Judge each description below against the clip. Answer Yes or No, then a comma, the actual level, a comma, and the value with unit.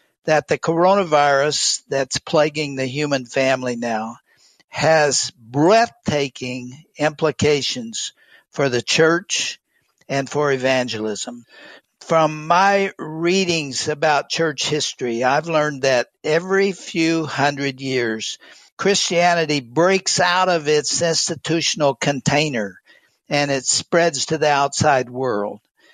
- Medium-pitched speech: Yes, medium, 150 Hz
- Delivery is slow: Yes, slow, 105 wpm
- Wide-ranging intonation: No, average, 3.9 semitones